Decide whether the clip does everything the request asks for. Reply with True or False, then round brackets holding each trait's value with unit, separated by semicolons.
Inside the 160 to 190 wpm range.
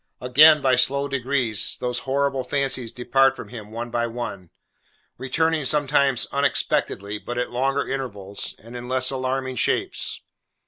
False (140 wpm)